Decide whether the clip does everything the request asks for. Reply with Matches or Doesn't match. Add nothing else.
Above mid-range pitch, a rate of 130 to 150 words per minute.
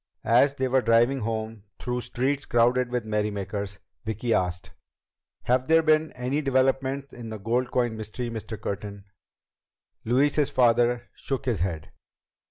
Doesn't match